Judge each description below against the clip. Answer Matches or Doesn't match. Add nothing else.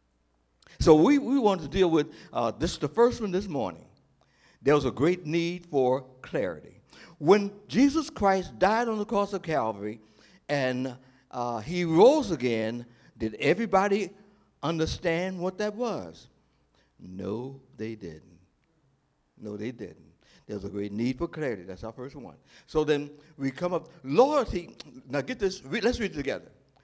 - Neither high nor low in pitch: Matches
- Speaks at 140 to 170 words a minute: Matches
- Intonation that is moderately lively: Doesn't match